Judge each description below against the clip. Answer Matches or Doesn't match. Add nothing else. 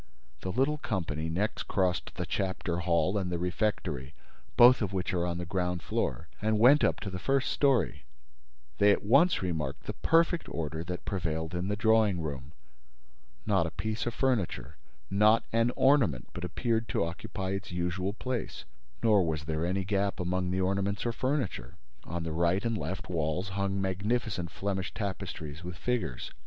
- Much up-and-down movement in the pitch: Doesn't match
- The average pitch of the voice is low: Matches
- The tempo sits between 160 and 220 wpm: Matches